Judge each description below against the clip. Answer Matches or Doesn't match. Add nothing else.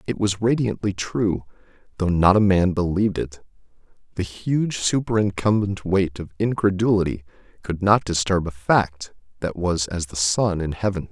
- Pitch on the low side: Matches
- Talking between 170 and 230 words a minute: Doesn't match